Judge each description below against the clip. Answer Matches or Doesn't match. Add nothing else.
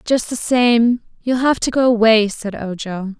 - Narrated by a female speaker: Matches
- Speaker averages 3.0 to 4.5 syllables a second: Matches